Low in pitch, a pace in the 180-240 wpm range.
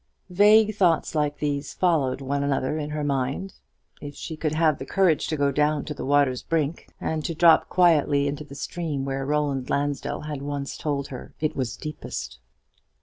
No: medium, 145 Hz; average, 185 wpm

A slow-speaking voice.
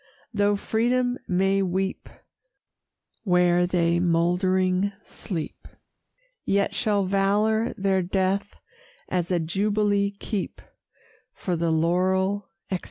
Yes: slow, 100 wpm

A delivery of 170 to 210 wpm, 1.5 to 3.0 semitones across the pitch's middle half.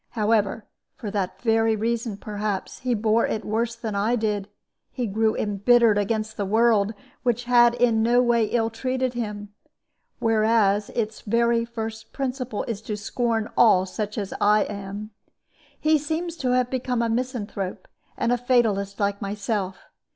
No: average, 155 wpm; narrow, 2.5 semitones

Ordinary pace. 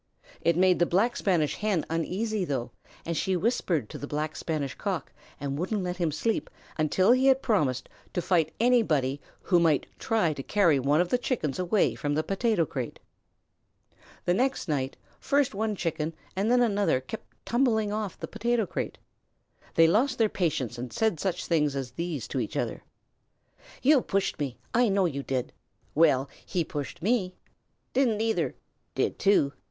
Yes: average, 170 wpm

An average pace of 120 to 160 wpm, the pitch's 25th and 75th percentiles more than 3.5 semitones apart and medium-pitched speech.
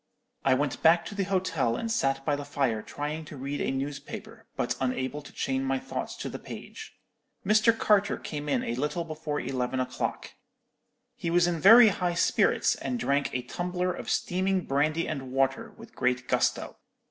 No: average, 180 wpm; average, 4.9 semitones; medium, 145 Hz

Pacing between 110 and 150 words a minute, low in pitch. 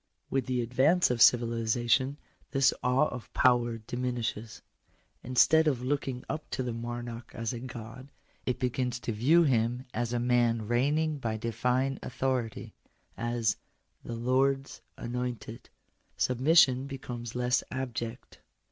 Yes: slow, 135 wpm; low, 125 Hz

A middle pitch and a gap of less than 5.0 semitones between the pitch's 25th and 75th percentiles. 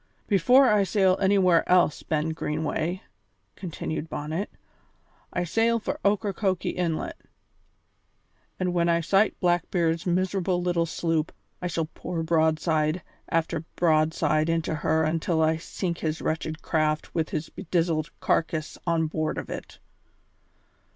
Yes: medium, 165 Hz; narrow, 2.4 semitones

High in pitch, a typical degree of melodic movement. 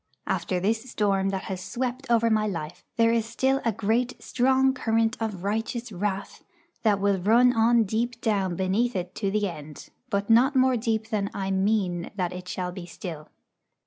Yes: high, 215 Hz; average, 3.5 semitones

